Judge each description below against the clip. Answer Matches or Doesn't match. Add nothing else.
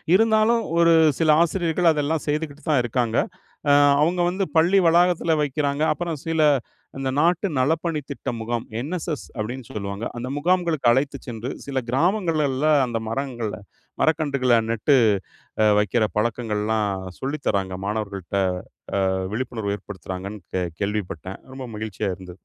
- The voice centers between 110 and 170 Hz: Matches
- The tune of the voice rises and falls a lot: Matches